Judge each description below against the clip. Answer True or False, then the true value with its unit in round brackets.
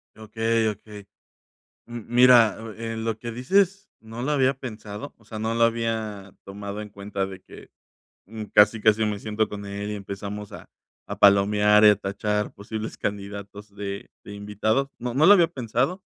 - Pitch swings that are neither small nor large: False (2.2 semitones)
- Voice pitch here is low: True (110 Hz)